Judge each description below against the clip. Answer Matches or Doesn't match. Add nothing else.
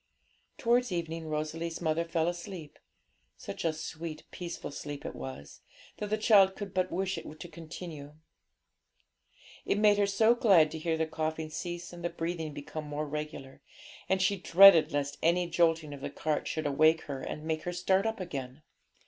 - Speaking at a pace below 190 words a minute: Matches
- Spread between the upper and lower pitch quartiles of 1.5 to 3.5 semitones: Matches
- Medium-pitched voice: Matches